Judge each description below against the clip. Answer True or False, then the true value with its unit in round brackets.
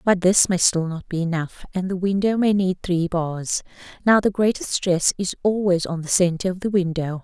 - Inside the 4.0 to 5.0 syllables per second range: True (4.9 syllables/s)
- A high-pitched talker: False (180 Hz)